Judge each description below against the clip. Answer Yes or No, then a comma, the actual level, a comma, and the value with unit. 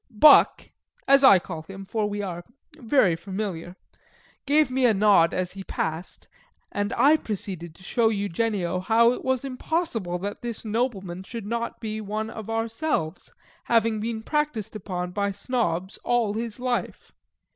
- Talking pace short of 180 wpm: Yes, average, 155 wpm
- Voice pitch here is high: Yes, high, 215 Hz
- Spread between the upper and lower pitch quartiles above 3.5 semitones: Yes, average, 3.9 semitones